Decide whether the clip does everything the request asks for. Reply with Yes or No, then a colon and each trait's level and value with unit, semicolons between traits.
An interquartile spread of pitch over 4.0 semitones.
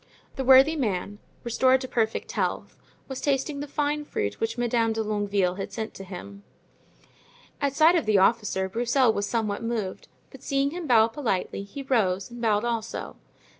Yes: average, 4.6 semitones